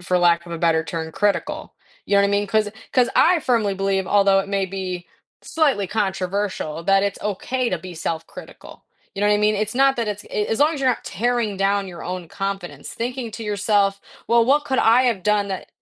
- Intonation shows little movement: No, average, 3.2 semitones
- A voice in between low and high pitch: No, high, 200 Hz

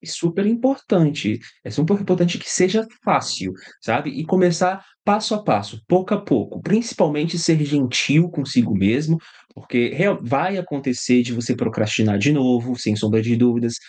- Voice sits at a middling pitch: Yes, medium, 145 Hz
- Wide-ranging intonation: Yes, wide, 7.4 semitones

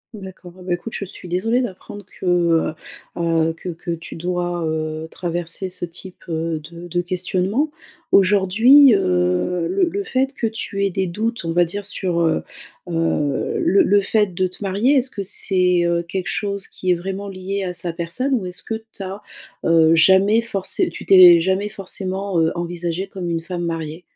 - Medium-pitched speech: Yes, medium, 180 Hz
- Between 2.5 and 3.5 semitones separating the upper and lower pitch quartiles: Yes, average, 2.8 semitones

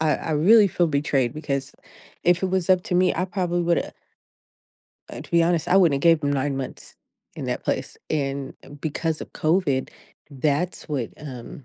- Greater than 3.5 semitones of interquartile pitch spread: Yes, average, 3.9 semitones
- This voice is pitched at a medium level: Yes, medium, 155 Hz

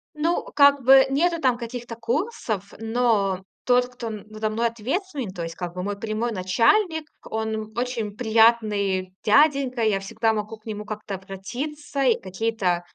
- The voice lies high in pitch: Yes, high, 225 Hz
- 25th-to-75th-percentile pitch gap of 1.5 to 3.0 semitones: No, average, 3.7 semitones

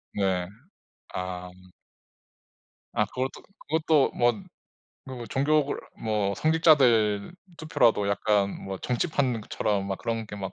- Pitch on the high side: No, low, 115 Hz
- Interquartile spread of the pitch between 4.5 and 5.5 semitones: Yes, average, 5.2 semitones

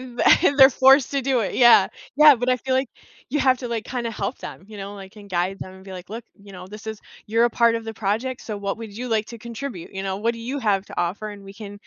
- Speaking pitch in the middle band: No, high, 225 Hz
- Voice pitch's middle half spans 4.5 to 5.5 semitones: No, average, 3.8 semitones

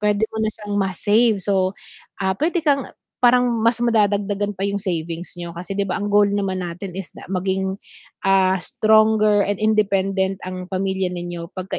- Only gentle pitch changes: Yes, narrow, 2.1 semitones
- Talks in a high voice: Yes, high, 195 Hz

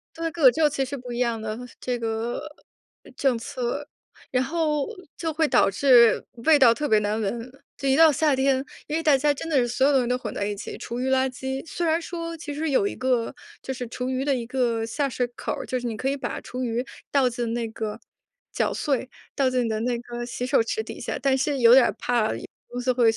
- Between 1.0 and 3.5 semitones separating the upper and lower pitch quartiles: Yes, average, 3.0 semitones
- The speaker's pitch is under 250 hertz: No, very high, 255 Hz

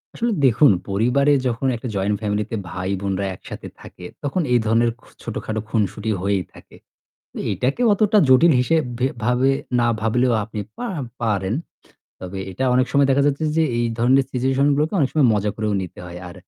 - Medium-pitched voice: No, low, 120 Hz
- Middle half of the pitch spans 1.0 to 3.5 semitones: No, average, 4.9 semitones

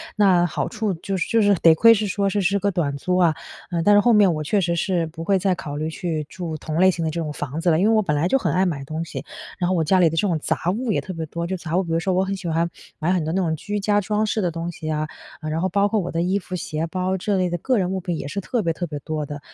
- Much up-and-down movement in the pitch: No, average, 3.4 semitones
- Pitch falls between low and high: Yes, medium, 175 Hz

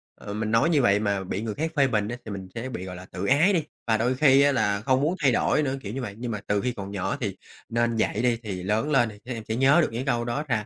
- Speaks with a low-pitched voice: Yes, low, 115 Hz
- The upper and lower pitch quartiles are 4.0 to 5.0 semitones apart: Yes, average, 4.6 semitones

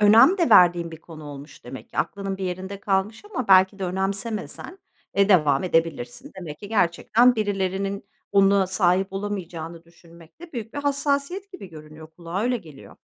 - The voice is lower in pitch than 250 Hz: Yes, high, 190 Hz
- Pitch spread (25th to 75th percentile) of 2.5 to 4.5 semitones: Yes, average, 3.9 semitones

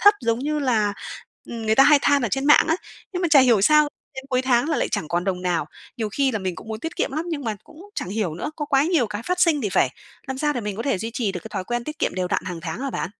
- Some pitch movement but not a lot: No, wide, 6.2 semitones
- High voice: Yes, high, 245 Hz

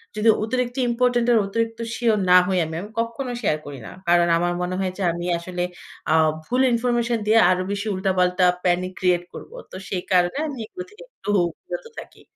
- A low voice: No, high, 205 Hz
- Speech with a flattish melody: No, average, 4.9 semitones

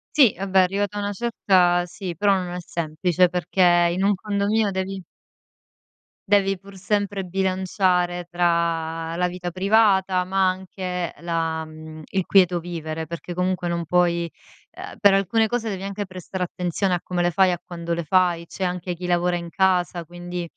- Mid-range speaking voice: Yes, medium, 180 Hz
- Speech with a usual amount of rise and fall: No, narrow, 2.0 semitones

